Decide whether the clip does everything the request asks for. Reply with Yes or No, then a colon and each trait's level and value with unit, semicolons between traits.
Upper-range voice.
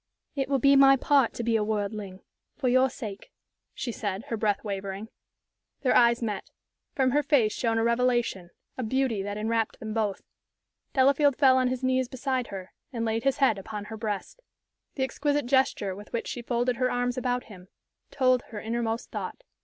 Yes: high, 235 Hz